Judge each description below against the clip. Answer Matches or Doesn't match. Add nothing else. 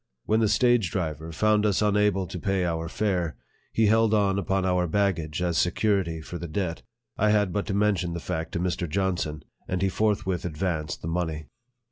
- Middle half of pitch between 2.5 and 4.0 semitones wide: Matches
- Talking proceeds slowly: Doesn't match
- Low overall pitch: Matches